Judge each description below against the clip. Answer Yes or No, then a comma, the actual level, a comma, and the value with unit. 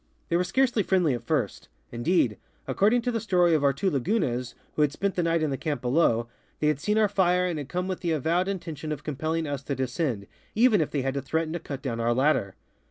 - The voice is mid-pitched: Yes, medium, 155 Hz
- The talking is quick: Yes, fast, 245 wpm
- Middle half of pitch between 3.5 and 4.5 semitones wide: No, average, 5.1 semitones